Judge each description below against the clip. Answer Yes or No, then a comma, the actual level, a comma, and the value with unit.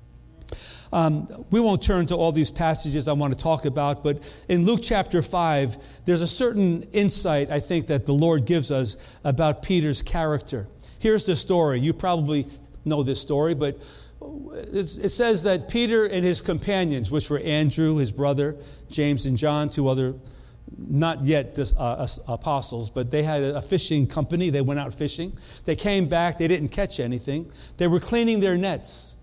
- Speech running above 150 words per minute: Yes, average, 175 wpm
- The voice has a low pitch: No, medium, 150 Hz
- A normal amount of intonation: Yes, average, 4.0 semitones